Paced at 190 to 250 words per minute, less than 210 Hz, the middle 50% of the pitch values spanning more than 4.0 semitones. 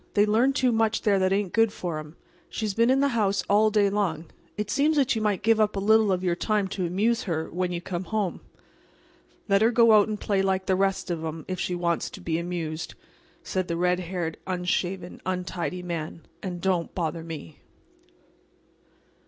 No: average, 200 wpm; high, 190 Hz; average, 3.4 semitones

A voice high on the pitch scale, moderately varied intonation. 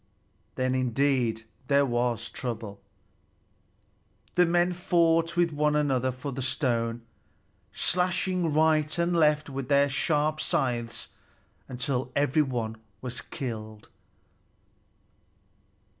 No: medium, 140 Hz; average, 4.2 semitones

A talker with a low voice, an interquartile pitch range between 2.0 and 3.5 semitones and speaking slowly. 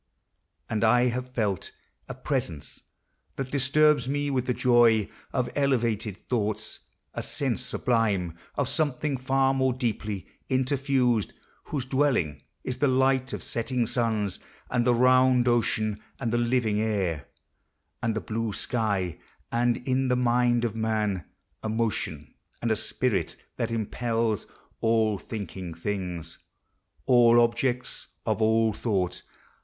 Yes: low, 120 Hz; average, 2.9 semitones; slow, 130 wpm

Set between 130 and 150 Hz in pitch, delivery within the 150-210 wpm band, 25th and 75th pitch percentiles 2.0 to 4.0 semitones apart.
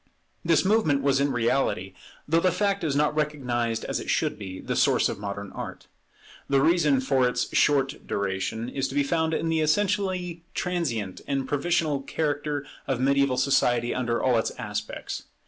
No: medium, 140 Hz; average, 170 wpm; average, 4.8 semitones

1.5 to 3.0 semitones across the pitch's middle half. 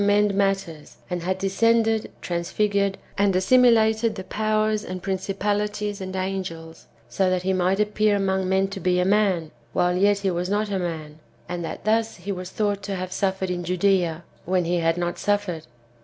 Yes: narrow, 2.4 semitones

